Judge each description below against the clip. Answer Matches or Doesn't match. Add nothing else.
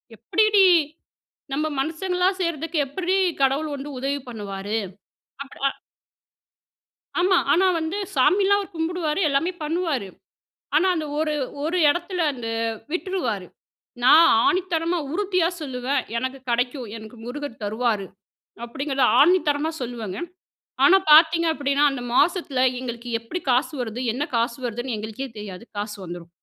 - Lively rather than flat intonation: Matches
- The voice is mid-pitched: Doesn't match